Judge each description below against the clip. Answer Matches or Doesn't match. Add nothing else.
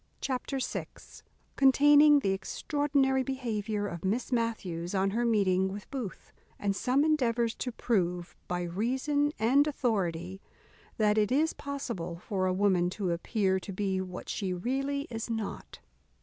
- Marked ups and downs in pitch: Matches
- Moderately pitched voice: Doesn't match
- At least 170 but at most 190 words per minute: Doesn't match